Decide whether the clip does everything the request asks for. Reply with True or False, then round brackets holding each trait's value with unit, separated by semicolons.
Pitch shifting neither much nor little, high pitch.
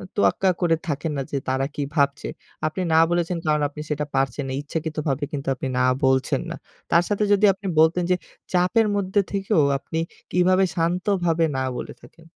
False (4.1 semitones; 165 Hz)